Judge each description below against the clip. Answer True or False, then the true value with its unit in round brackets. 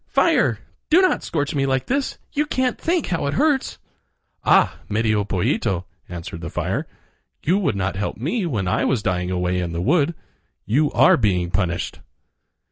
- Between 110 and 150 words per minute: False (170 wpm)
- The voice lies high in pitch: False (110 Hz)